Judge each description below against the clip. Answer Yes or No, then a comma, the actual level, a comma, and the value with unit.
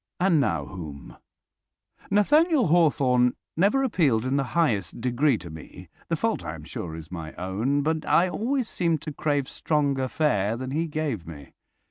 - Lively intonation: Yes, wide, 8.1 semitones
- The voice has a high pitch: No, medium, 140 Hz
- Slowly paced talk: No, average, 165 wpm